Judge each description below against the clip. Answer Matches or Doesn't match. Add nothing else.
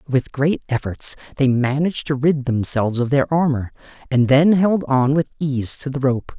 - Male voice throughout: Matches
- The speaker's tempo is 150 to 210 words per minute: Matches